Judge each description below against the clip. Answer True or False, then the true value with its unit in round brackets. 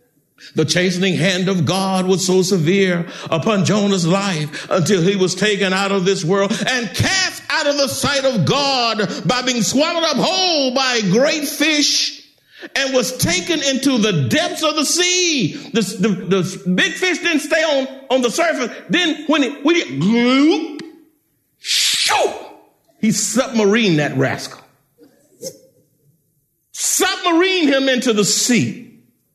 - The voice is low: False (235 Hz)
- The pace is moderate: True (155 wpm)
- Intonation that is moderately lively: False (7.6 semitones)